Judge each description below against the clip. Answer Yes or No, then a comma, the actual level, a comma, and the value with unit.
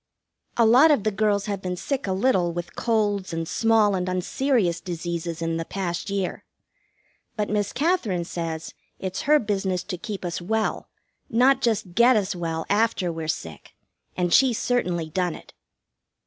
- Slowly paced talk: No, average, 165 wpm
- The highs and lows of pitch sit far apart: No, average, 4.4 semitones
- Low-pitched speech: No, high, 195 Hz